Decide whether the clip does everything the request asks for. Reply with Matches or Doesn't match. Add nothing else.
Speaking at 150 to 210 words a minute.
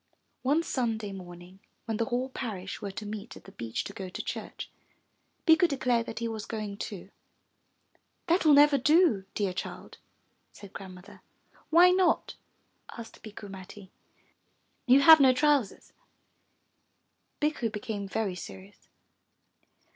Doesn't match